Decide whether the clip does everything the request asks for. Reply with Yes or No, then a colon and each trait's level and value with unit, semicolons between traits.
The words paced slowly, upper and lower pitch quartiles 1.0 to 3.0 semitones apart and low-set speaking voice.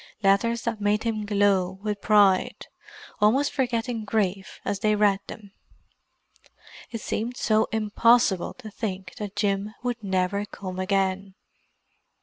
No: slow, 125 wpm; narrow, 2.5 semitones; high, 210 Hz